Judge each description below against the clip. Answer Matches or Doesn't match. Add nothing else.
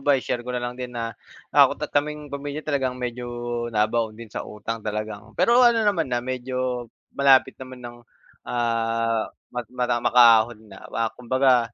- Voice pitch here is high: Doesn't match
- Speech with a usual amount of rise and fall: Doesn't match